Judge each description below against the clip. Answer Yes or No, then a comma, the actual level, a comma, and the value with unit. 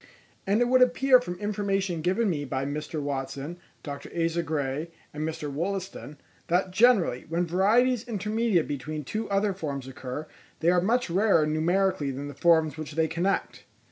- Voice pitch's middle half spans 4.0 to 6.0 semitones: Yes, average, 5.0 semitones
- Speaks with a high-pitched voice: No, medium, 170 Hz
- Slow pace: No, average, 165 wpm